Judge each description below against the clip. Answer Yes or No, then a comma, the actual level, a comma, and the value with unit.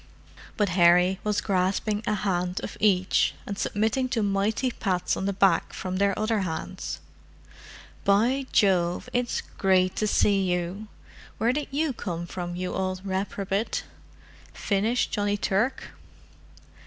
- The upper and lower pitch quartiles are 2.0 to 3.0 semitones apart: Yes, narrow, 2.6 semitones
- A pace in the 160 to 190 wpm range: No, slow, 135 wpm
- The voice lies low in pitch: No, high, 200 Hz